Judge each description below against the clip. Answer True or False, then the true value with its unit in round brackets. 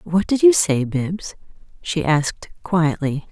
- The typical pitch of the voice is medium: True (170 Hz)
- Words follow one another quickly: False (145 wpm)